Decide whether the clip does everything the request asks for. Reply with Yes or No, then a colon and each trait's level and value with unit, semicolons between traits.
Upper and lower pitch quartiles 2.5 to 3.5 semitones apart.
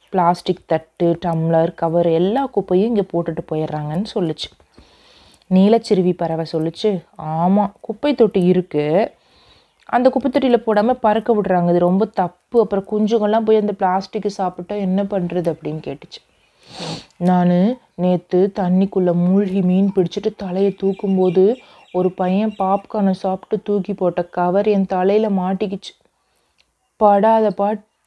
Yes: average, 2.9 semitones